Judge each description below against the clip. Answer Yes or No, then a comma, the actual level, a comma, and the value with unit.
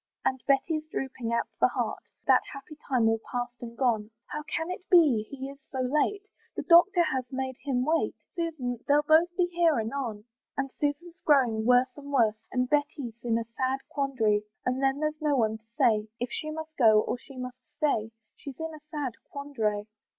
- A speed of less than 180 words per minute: No, average, 195 wpm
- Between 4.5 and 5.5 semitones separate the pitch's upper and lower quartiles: No, average, 4.1 semitones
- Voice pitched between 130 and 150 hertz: No, very high, 270 Hz